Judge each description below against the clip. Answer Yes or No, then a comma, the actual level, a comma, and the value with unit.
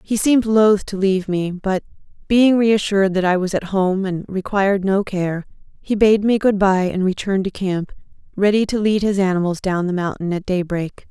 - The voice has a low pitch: No, high, 195 Hz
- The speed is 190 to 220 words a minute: Yes, average, 200 wpm